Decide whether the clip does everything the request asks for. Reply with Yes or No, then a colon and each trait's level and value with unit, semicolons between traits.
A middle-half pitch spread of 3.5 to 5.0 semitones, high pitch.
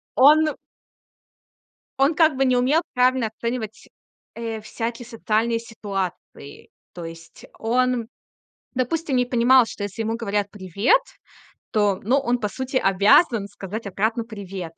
Yes: average, 3.8 semitones; high, 230 Hz